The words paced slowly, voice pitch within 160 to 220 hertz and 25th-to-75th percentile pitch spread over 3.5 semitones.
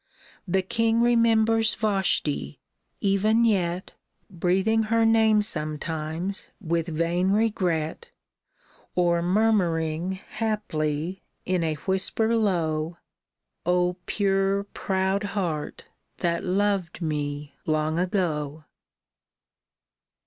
Yes: slow, 90 wpm; medium, 185 Hz; average, 4.5 semitones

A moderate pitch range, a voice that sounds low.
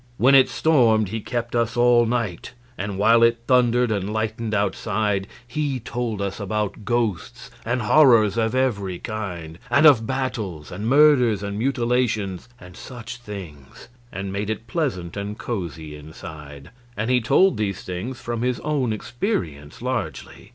Yes: average, 3.8 semitones; low, 110 Hz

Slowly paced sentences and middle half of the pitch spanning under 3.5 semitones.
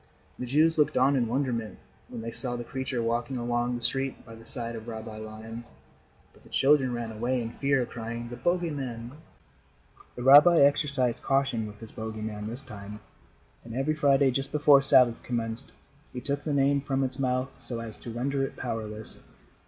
No: average, 190 wpm; average, 3.1 semitones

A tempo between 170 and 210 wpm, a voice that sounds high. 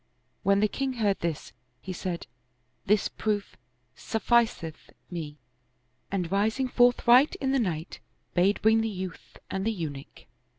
No: average, 140 wpm; high, 200 Hz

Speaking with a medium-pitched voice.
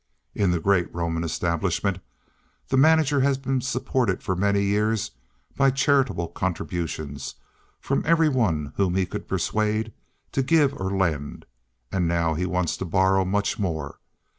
No: very low, 95 Hz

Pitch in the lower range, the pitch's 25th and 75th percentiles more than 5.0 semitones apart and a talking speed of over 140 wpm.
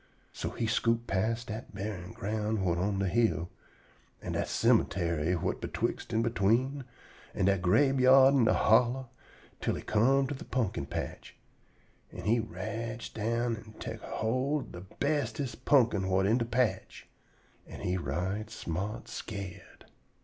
No: low, 110 Hz; average, 3.9 semitones; average, 150 wpm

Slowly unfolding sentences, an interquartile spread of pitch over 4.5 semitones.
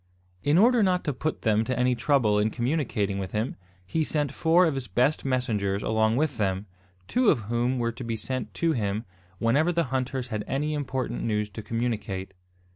No: average, 195 wpm; average, 5.1 semitones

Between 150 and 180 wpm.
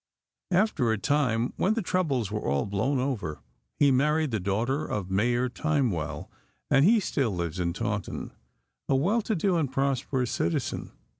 Yes: average, 160 wpm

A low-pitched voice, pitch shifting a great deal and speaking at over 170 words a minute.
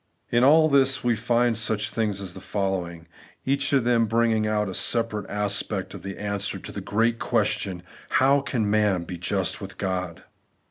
No: low, 110 Hz; average, 3.4 semitones; average, 185 wpm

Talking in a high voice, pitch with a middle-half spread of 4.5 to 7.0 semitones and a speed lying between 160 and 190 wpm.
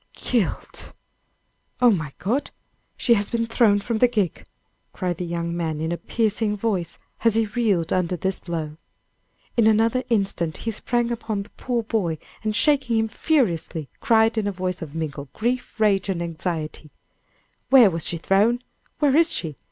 Yes: high, 205 Hz; average, 5.2 semitones; average, 165 wpm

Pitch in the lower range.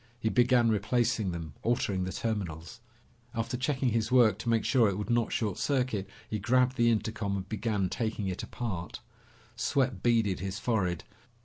Yes: low, 110 Hz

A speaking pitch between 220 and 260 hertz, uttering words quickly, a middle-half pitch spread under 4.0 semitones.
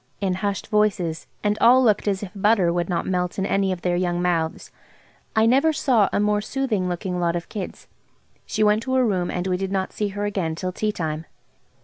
No: high, 195 Hz; fast, 220 wpm; average, 3.0 semitones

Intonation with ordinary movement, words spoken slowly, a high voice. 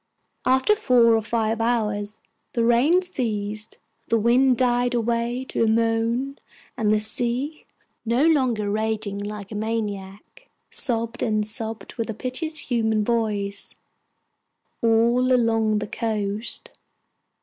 No: narrow, 2.3 semitones; slow, 125 wpm; high, 230 Hz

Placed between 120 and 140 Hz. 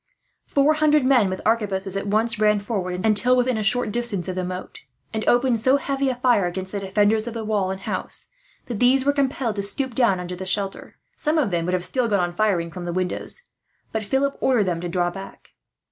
No: high, 210 Hz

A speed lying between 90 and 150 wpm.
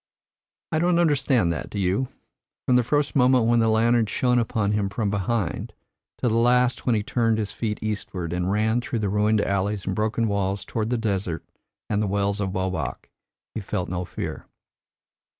No: average, 185 wpm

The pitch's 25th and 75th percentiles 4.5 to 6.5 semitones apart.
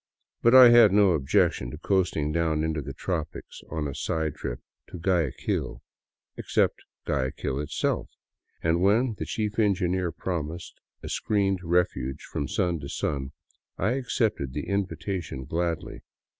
Yes: average, 5.0 semitones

